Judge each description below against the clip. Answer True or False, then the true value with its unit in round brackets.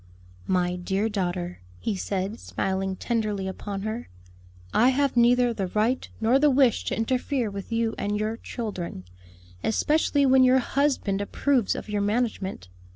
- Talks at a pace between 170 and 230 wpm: False (150 wpm)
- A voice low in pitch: False (220 Hz)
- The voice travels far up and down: False (4.3 semitones)